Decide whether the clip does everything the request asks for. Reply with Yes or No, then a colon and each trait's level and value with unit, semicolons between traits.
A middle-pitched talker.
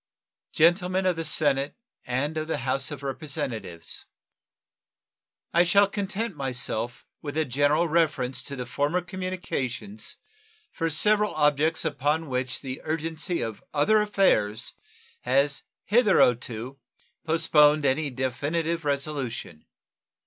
Yes: medium, 150 Hz